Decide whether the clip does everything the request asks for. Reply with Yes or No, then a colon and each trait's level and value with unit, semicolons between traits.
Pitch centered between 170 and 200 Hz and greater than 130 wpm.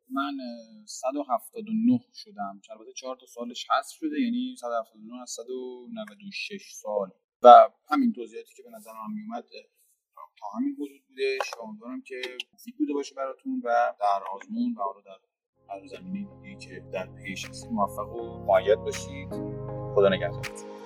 Yes: medium, 185 Hz; average, 140 wpm